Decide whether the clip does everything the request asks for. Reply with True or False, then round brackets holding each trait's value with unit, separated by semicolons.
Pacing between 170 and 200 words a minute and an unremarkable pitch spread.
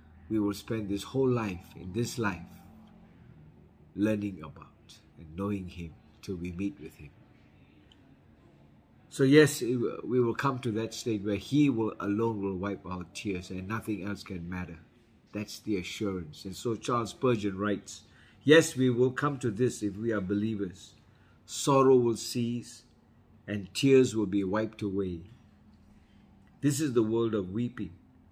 False (155 wpm; 3.6 semitones)